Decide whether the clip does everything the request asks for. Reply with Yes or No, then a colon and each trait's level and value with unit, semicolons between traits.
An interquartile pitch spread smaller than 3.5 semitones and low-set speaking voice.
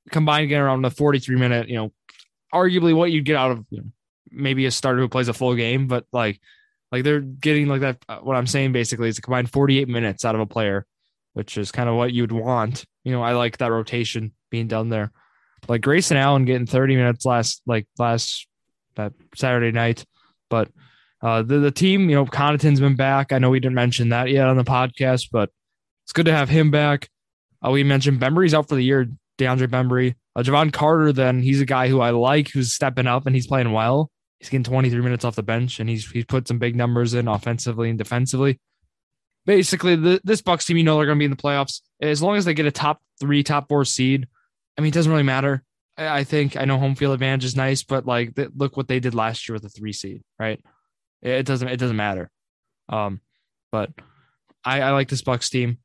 Yes: average, 2.9 semitones; low, 130 Hz